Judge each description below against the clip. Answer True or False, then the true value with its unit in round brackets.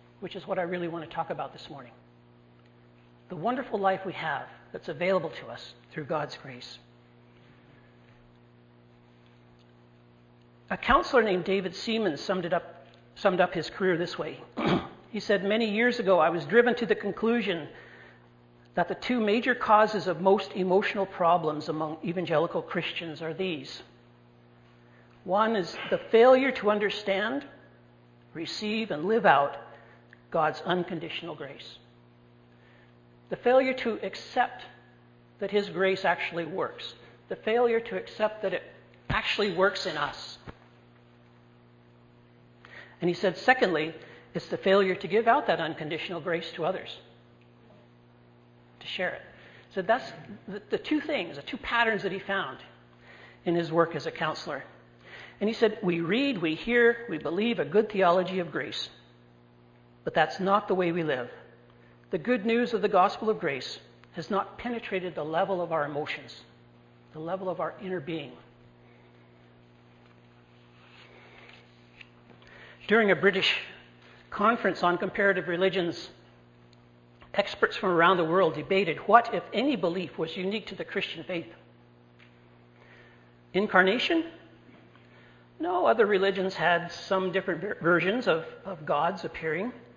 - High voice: False (165 Hz)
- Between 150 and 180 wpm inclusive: False (140 wpm)